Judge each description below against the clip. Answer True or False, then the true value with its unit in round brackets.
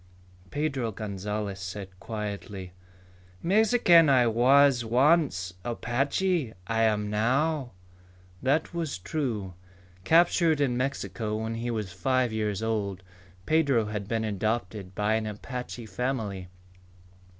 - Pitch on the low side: True (115 Hz)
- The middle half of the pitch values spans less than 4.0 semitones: False (4.8 semitones)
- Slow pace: True (110 wpm)